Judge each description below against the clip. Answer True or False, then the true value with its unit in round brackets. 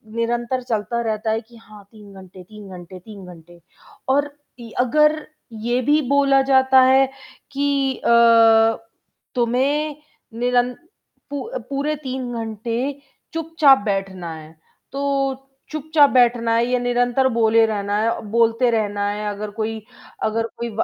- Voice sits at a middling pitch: False (235 Hz)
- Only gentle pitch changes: False (3.6 semitones)